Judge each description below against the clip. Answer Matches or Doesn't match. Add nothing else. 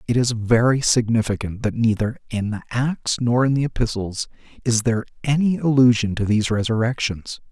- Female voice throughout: Doesn't match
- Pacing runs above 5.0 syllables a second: Matches